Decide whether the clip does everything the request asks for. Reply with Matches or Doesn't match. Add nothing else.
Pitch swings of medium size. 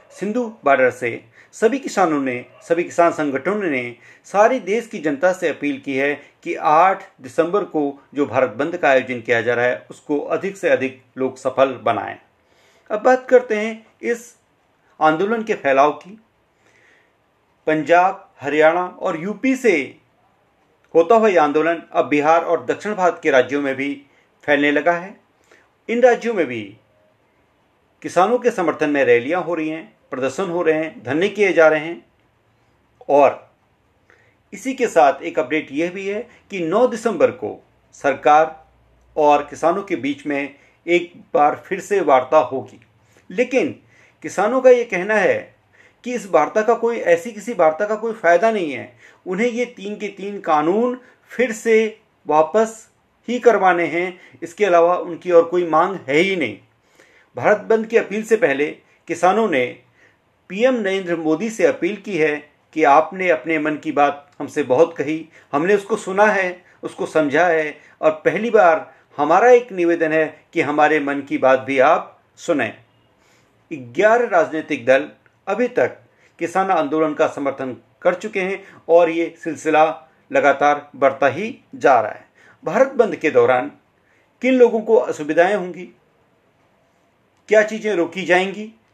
Doesn't match